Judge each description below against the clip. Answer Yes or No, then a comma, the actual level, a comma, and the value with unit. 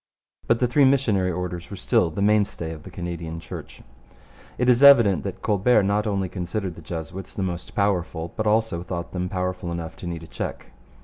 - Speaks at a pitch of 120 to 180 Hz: No, very low, 90 Hz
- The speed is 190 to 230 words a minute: Yes, average, 195 wpm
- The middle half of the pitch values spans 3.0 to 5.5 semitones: Yes, average, 3.5 semitones